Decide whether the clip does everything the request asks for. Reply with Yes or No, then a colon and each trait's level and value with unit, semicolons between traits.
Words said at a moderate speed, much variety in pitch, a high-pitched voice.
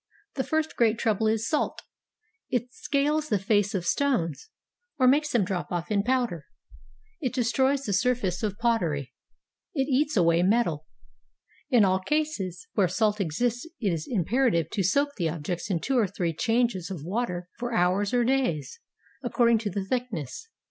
Yes: average, 170 wpm; wide, 5.8 semitones; high, 220 Hz